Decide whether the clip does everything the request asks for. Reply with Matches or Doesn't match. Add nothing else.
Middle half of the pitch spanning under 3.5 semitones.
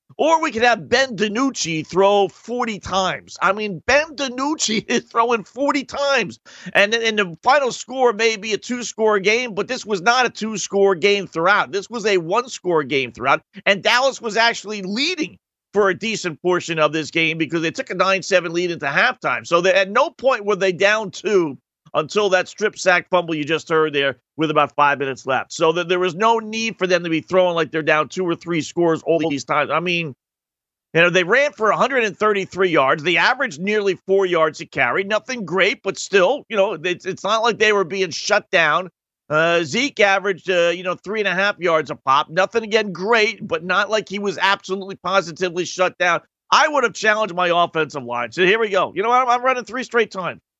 Doesn't match